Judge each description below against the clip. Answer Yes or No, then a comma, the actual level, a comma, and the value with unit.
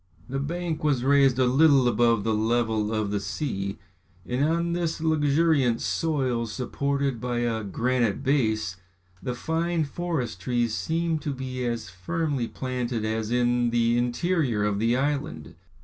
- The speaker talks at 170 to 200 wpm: No, average, 150 wpm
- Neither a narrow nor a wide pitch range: Yes, average, 4.3 semitones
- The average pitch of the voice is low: Yes, low, 125 Hz